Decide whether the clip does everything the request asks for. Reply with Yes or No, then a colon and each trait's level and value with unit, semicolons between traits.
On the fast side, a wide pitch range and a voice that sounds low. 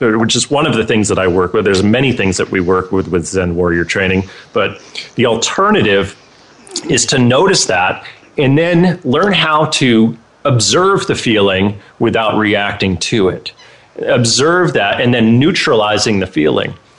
No: average, 165 wpm; wide, 5.7 semitones; low, 110 Hz